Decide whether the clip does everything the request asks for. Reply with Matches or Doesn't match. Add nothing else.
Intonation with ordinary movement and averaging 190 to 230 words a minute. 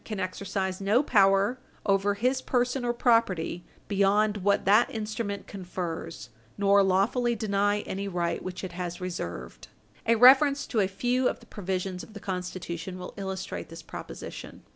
Doesn't match